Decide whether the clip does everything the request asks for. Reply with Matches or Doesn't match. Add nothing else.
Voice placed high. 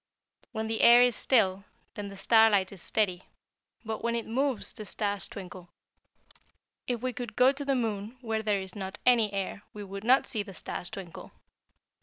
Matches